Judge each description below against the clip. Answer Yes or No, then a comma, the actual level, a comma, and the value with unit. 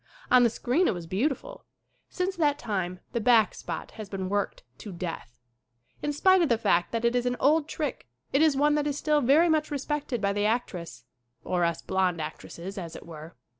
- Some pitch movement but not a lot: No, wide, 8.1 semitones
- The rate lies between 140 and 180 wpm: No, fast, 205 wpm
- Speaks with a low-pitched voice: No, high, 235 Hz